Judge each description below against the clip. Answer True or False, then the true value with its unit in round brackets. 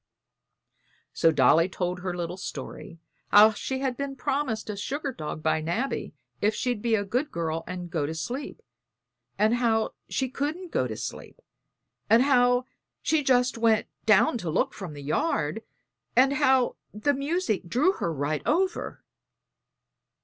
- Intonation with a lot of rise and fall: True (7.4 semitones)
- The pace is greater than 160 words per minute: False (155 wpm)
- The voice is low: False (225 Hz)